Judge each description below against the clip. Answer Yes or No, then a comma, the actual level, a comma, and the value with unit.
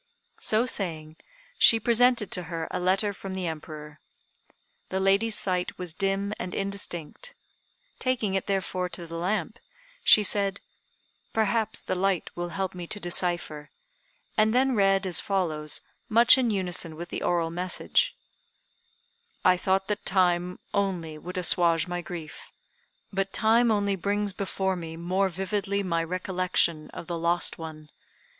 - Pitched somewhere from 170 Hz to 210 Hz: Yes, medium, 185 Hz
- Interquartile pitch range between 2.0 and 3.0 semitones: Yes, average, 2.7 semitones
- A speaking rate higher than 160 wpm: No, average, 145 wpm